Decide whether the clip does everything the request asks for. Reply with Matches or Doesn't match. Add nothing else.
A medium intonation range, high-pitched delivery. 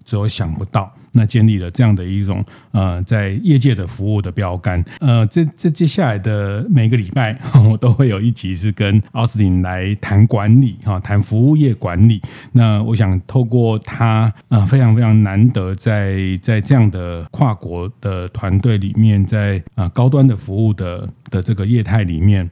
Doesn't match